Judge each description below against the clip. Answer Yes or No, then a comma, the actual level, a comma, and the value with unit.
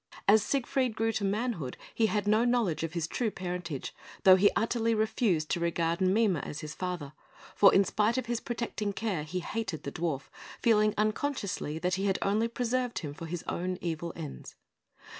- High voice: Yes, high, 200 Hz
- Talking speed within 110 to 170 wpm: No, average, 185 wpm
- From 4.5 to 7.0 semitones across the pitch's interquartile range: Yes, average, 5.0 semitones